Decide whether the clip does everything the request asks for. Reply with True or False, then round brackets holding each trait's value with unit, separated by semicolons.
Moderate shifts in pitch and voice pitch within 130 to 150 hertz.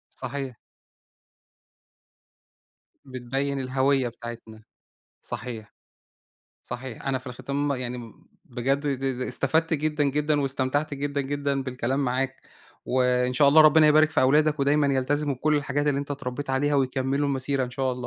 False (2.1 semitones; 135 Hz)